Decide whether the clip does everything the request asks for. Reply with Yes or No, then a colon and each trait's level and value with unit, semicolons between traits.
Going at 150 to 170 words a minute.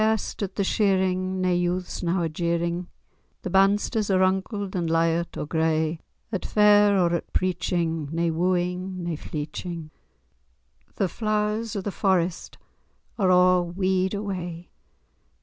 No: average, 140 wpm